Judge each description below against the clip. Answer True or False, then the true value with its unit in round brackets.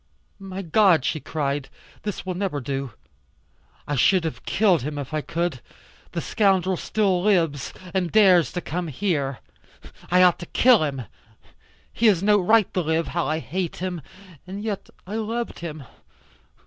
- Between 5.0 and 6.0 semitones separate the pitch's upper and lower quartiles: False (4.2 semitones)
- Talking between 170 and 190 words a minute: False (160 wpm)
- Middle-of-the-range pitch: True (175 Hz)